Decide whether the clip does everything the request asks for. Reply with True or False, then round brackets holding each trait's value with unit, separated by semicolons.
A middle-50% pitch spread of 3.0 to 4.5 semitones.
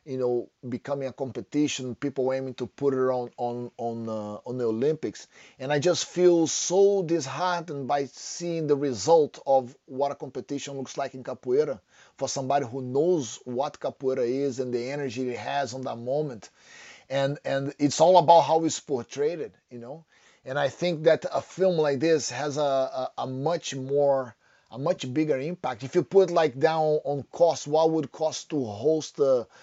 True (3.6 semitones)